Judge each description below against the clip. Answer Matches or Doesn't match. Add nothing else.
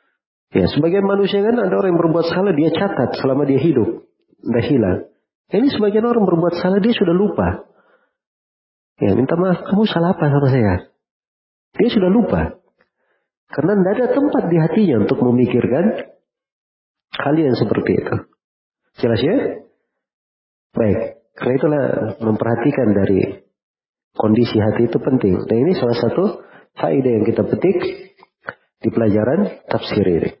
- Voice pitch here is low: Doesn't match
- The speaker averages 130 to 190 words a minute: Matches